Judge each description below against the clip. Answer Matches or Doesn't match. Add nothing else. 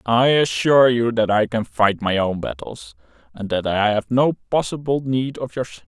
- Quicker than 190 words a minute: Matches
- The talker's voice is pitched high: Doesn't match